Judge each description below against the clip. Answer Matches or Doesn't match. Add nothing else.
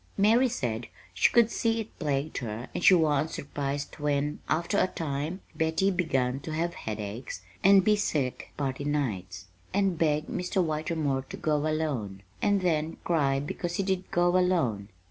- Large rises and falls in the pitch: Doesn't match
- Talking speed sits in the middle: Matches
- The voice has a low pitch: Doesn't match